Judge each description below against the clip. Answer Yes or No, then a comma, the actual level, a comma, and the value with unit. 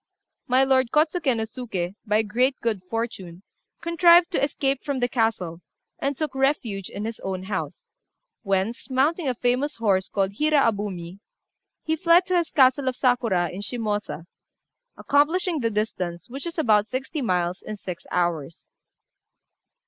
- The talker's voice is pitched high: Yes, high, 235 Hz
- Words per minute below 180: Yes, average, 150 wpm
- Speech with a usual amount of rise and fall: No, wide, 6.3 semitones